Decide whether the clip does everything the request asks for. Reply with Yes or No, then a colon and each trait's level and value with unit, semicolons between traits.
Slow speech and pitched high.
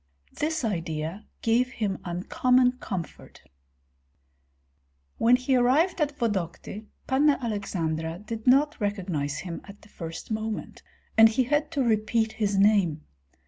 Yes: slow, 125 wpm; high, 220 Hz